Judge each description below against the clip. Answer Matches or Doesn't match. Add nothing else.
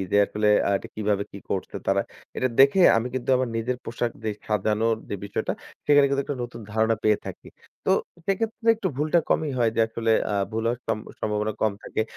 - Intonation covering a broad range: Doesn't match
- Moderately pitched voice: Doesn't match